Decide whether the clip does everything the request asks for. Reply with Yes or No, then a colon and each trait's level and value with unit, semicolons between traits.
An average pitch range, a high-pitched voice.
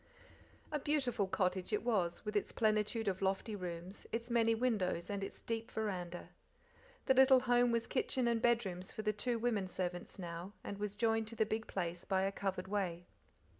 Yes: average, 3.7 semitones; high, 210 Hz